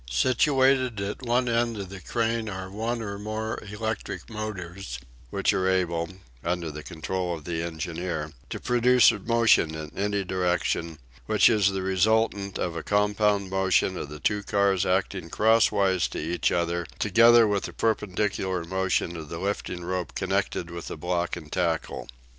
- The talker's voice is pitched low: Yes, very low, 95 Hz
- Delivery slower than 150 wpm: No, average, 165 wpm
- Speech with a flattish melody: No, average, 3.8 semitones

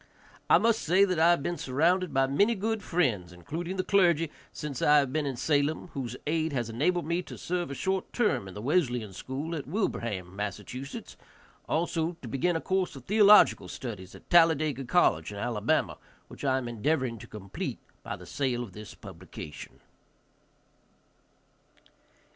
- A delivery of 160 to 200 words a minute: Yes, average, 170 wpm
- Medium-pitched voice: Yes, medium, 145 Hz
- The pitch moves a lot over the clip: Yes, wide, 6.6 semitones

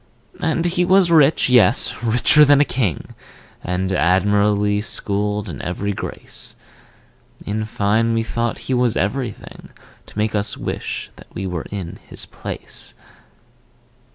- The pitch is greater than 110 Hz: No, low, 105 Hz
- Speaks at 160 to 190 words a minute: No, average, 140 wpm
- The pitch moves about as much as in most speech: Yes, average, 3.8 semitones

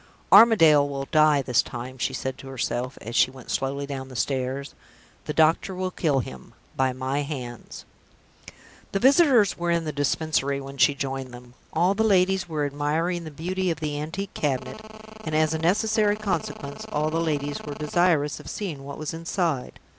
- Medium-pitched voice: Yes, medium, 150 Hz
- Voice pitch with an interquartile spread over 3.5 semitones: Yes, average, 4.2 semitones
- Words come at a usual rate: Yes, average, 180 wpm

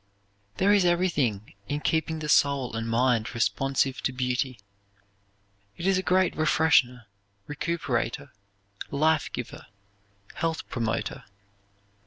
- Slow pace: Yes, slow, 110 wpm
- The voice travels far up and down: No, average, 4.5 semitones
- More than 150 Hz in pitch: No, medium, 140 Hz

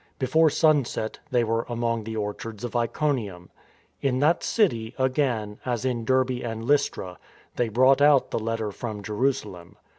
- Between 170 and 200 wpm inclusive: No, average, 150 wpm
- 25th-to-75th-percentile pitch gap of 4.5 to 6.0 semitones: No, average, 3.2 semitones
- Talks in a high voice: No, low, 120 Hz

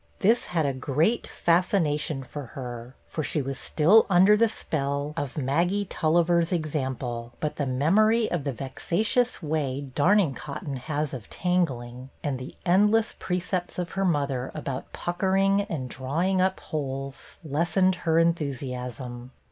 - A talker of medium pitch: Yes, medium, 155 Hz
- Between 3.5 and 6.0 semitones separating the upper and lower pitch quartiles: Yes, average, 5.1 semitones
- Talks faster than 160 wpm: No, average, 155 wpm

